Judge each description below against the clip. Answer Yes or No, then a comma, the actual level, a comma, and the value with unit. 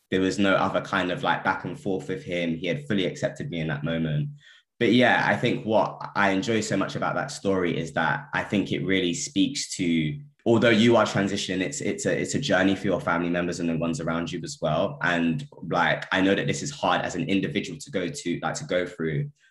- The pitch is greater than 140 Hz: No, very low, 90 Hz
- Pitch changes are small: No, average, 3.0 semitones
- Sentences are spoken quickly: Yes, fast, 245 wpm